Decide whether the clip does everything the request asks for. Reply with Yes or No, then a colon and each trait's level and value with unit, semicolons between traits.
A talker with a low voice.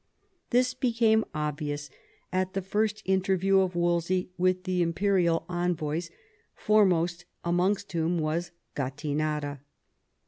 No: medium, 180 Hz